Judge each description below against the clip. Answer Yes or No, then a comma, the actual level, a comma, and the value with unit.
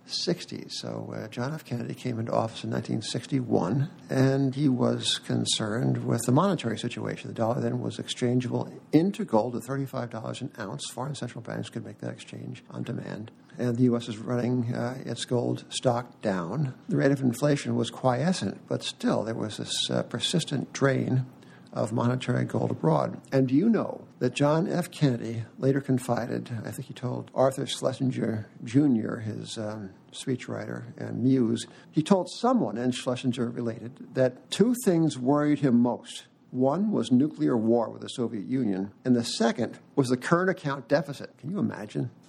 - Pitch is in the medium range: No, low, 125 Hz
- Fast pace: No, average, 170 wpm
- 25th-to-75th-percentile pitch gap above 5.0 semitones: No, average, 3.2 semitones